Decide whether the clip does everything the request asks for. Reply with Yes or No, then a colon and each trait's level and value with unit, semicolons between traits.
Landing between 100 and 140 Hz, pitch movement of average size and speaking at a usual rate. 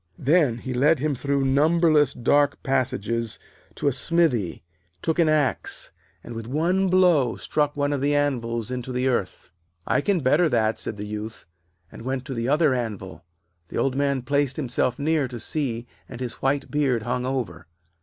Yes: low, 135 Hz; average, 3.5 semitones; average, 175 wpm